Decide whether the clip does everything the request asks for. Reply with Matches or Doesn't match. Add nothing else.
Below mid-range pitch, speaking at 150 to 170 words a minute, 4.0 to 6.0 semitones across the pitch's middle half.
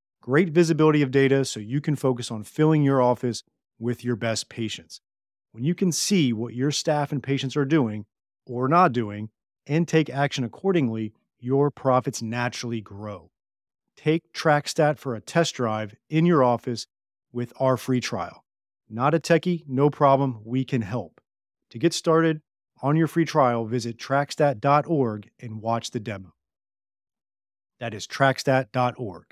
Matches